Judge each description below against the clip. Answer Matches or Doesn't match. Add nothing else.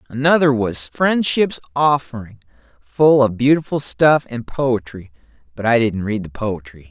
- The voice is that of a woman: Doesn't match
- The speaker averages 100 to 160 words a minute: Matches